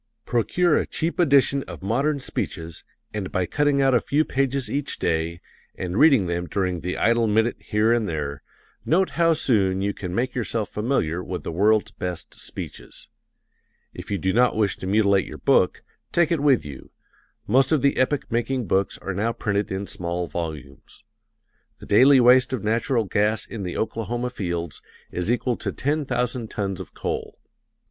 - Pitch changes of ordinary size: No, wide, 5.8 semitones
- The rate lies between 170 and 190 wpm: Yes, average, 175 wpm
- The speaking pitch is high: No, low, 110 Hz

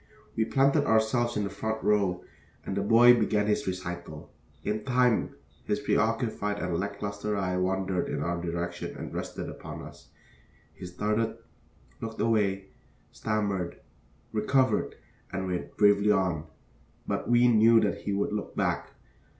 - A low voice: Yes, low, 105 Hz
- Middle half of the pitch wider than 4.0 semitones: No, average, 2.9 semitones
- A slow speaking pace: No, average, 145 wpm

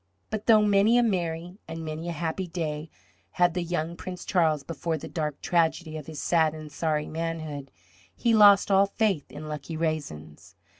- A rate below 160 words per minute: No, average, 180 wpm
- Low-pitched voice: No, medium, 165 Hz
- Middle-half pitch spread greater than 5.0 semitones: No, average, 2.9 semitones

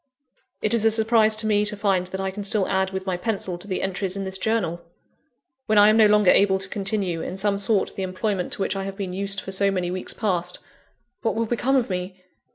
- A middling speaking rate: No, fast, 245 wpm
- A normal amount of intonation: No, narrow, 2.3 semitones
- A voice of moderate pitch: No, high, 195 Hz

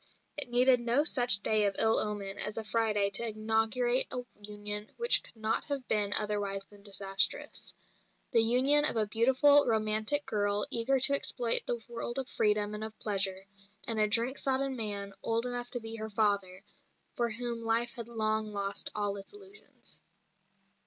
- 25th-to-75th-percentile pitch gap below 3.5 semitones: Yes, average, 2.8 semitones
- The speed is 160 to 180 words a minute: Yes, average, 175 wpm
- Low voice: No, high, 220 Hz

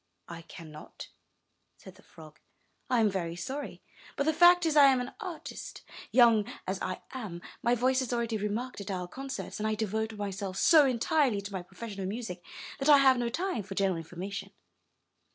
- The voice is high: Yes, high, 220 Hz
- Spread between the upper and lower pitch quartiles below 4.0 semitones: No, wide, 5.5 semitones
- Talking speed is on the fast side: No, average, 190 wpm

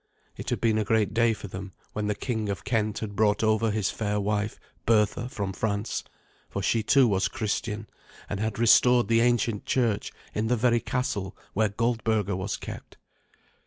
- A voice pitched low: Yes, low, 110 Hz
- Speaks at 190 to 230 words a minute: No, average, 180 wpm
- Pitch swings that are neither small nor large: No, narrow, 2.1 semitones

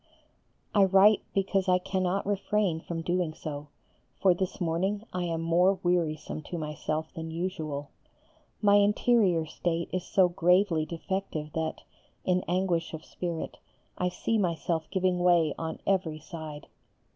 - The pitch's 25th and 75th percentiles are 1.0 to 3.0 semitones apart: Yes, average, 2.7 semitones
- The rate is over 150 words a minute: No, average, 140 wpm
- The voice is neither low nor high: Yes, medium, 175 Hz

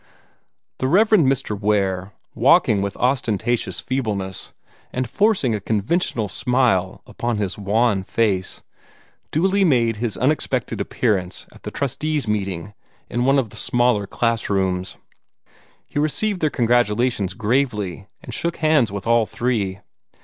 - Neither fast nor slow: No, slow, 125 wpm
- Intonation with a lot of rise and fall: No, average, 4.7 semitones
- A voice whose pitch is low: Yes, low, 115 Hz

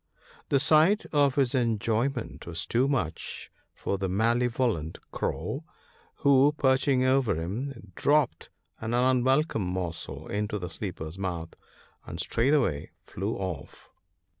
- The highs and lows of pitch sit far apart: Yes, wide, 6.3 semitones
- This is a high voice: No, low, 115 Hz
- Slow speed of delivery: Yes, slow, 125 wpm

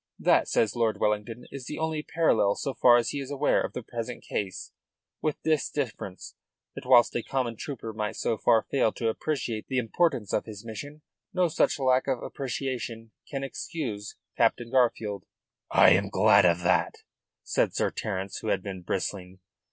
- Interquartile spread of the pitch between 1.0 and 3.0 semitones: No, average, 4.5 semitones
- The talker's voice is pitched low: Yes, low, 115 Hz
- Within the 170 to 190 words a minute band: Yes, average, 175 wpm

